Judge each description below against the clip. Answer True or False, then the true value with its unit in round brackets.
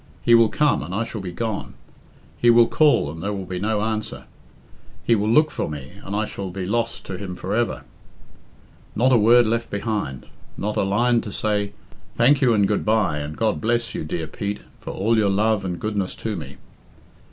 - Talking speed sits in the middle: False (210 wpm)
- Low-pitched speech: True (105 Hz)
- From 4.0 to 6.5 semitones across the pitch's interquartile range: False (3.2 semitones)